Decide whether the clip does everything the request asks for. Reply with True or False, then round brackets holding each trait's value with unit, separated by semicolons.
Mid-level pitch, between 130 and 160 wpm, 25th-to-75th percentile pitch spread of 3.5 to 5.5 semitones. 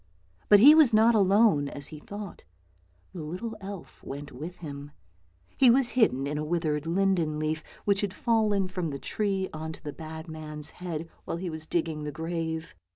False (165 Hz; 185 wpm; 4.7 semitones)